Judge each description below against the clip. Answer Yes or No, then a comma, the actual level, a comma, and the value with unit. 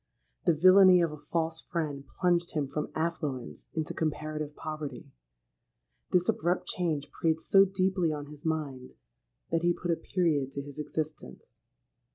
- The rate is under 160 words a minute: Yes, average, 150 wpm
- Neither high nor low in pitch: Yes, medium, 160 Hz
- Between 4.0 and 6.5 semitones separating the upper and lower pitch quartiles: No, average, 2.8 semitones